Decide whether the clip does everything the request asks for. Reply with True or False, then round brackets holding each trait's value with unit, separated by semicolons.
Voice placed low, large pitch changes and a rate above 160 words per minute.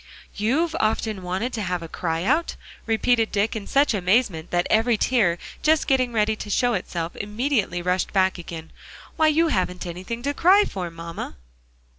False (210 Hz; 5.7 semitones; 170 wpm)